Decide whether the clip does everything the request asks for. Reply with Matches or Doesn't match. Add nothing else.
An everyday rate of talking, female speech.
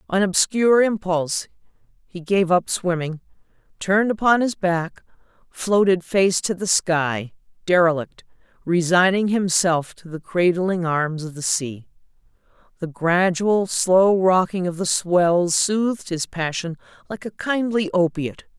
Doesn't match